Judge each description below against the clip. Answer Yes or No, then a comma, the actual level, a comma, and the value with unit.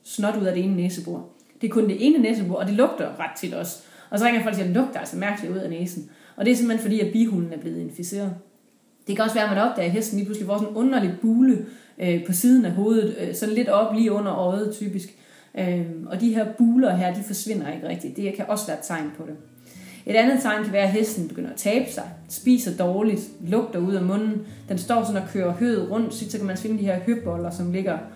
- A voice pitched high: Yes, high, 210 Hz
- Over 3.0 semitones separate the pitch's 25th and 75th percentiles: Yes, average, 3.5 semitones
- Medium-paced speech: No, fast, 260 wpm